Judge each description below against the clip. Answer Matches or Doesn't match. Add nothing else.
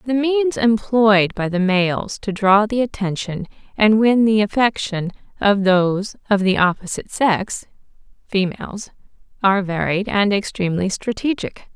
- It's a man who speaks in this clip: Doesn't match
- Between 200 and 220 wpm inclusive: Doesn't match